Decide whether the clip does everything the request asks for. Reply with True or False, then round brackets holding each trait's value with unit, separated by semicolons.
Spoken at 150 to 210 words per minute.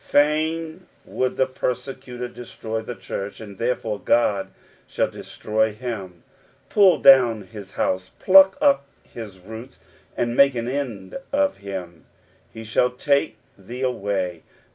False (135 wpm)